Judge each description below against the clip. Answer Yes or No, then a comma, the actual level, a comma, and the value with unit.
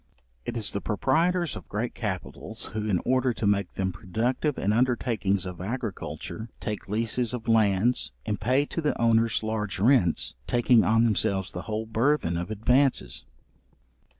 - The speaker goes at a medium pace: Yes, average, 155 wpm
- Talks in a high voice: No, low, 110 Hz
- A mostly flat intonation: No, average, 3.7 semitones